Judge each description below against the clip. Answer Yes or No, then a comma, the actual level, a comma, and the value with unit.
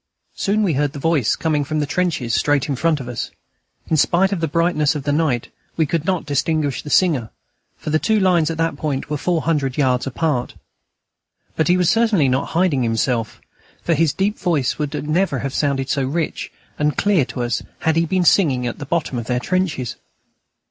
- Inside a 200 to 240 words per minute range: Yes, fast, 205 wpm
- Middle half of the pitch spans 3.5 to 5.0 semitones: Yes, average, 3.8 semitones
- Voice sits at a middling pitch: Yes, medium, 150 Hz